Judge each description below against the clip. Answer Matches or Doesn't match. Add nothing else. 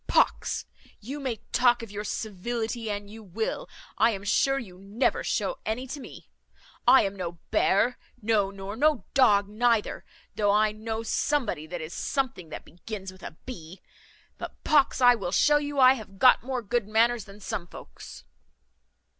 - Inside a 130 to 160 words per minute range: Doesn't match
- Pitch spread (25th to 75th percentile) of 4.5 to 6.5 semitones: Doesn't match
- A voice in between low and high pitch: Doesn't match